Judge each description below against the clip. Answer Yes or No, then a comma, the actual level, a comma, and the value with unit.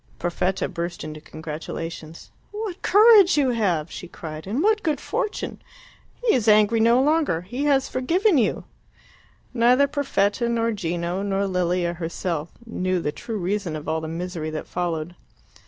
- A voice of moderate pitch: No, high, 195 Hz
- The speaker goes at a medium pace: Yes, average, 155 wpm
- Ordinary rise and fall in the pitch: No, wide, 7.3 semitones